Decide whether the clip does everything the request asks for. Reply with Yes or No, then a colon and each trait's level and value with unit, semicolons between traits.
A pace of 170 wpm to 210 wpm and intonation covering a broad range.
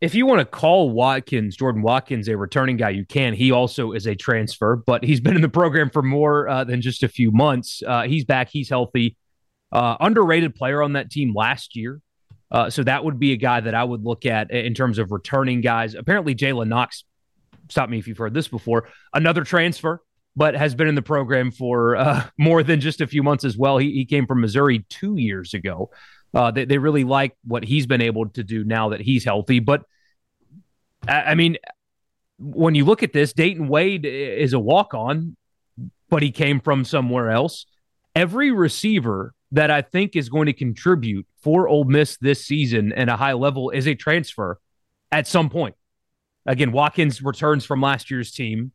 No: average, 200 wpm; average, 4.2 semitones